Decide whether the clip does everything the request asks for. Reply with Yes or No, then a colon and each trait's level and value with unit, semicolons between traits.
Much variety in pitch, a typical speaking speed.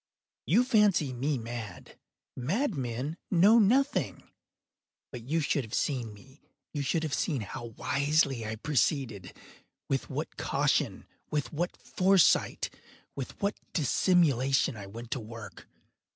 No: wide, 6.0 semitones; slow, 115 wpm